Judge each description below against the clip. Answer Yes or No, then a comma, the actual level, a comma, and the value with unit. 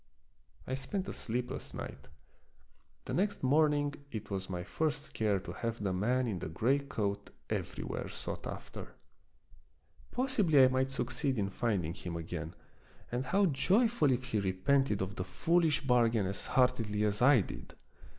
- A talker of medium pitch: No, low, 125 Hz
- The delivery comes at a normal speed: Yes, average, 155 wpm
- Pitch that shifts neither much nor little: No, wide, 6.1 semitones